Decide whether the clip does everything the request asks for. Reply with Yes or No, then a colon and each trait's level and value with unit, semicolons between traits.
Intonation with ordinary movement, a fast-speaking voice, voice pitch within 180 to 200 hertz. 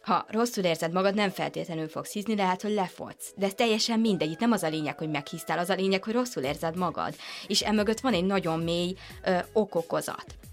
Yes: average, 4.5 semitones; fast, 210 wpm; high, 190 Hz